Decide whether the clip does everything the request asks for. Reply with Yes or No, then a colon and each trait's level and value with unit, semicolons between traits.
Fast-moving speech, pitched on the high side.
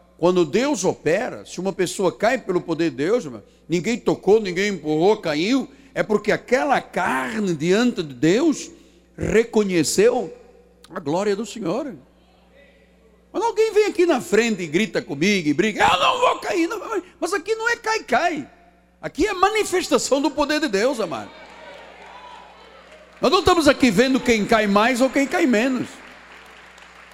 No: average, 155 wpm; high, 240 Hz